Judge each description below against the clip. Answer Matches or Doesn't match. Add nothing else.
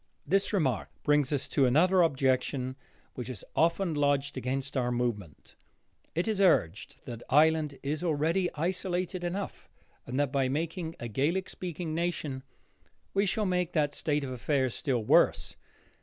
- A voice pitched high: Doesn't match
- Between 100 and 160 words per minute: Matches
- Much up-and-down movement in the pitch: Doesn't match